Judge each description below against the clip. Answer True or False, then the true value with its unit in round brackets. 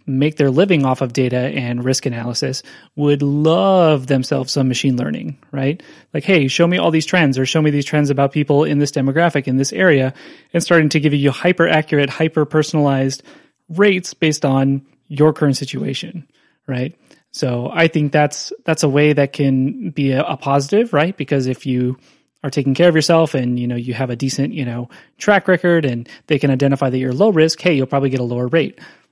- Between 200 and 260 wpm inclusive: True (205 wpm)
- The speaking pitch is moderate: True (145 Hz)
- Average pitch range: True (3.1 semitones)